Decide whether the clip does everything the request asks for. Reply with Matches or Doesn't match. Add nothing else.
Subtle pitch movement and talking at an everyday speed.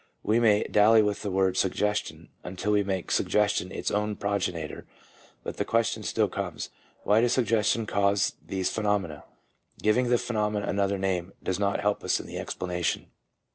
Matches